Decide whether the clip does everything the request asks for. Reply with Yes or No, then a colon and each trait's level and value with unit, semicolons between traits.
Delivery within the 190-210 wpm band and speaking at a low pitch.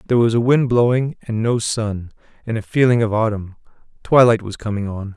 Yes: average, 200 wpm; low, 115 Hz